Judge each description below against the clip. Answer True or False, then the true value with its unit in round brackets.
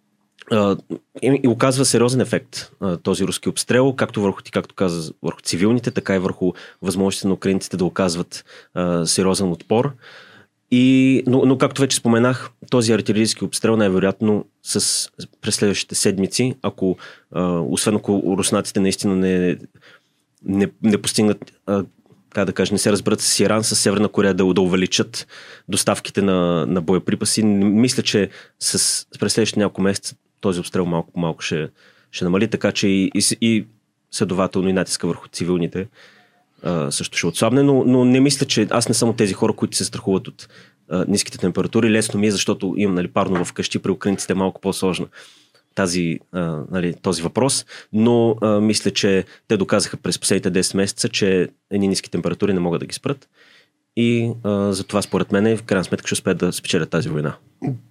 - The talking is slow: False (165 wpm)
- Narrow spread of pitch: False (3.2 semitones)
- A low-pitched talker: True (100 Hz)